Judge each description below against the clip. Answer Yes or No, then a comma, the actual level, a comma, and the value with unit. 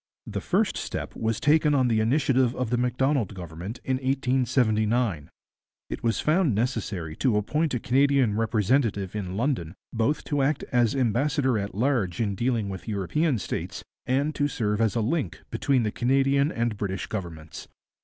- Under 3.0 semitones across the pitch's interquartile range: No, average, 4.4 semitones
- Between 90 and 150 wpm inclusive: No, average, 165 wpm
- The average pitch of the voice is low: Yes, low, 120 Hz